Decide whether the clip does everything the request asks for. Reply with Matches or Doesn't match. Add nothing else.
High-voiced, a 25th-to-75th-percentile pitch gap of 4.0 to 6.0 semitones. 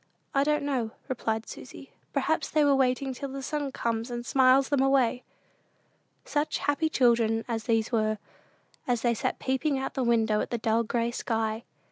Doesn't match